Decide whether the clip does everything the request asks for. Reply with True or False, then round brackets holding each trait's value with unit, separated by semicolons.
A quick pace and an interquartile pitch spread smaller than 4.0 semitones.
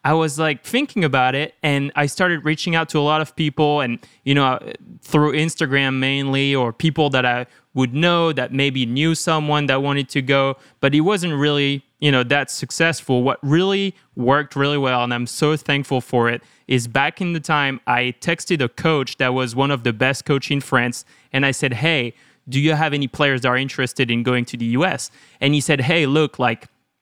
True (215 wpm; 3.1 semitones)